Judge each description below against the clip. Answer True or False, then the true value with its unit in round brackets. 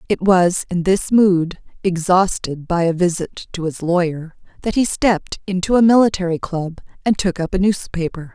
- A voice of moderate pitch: True (180 Hz)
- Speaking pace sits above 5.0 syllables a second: False (4.8 syllables/s)